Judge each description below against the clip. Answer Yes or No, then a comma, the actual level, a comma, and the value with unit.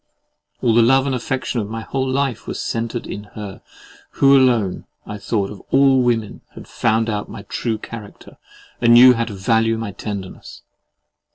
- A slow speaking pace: No, average, 175 wpm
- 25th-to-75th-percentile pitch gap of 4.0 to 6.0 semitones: No, average, 3.3 semitones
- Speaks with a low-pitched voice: Yes, low, 115 Hz